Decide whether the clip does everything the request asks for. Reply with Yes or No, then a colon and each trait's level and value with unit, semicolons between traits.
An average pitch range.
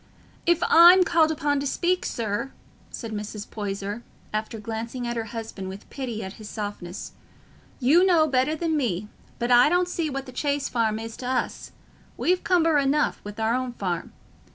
No: wide, 5.9 semitones